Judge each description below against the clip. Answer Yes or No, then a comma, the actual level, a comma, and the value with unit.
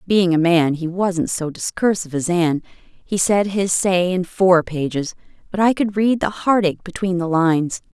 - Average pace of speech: Yes, average, 190 wpm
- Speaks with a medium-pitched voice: Yes, medium, 180 Hz